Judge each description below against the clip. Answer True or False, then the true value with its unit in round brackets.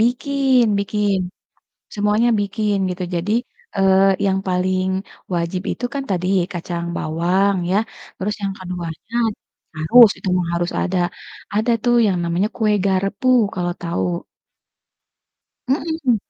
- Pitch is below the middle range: False (195 Hz)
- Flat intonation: False (3.5 semitones)